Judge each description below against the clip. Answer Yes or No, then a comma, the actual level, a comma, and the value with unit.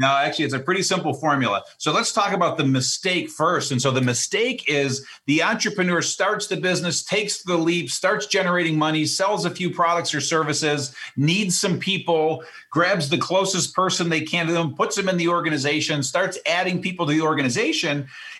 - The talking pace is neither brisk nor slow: Yes, average, 190 wpm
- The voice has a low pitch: No, medium, 170 Hz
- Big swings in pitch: No, average, 3.7 semitones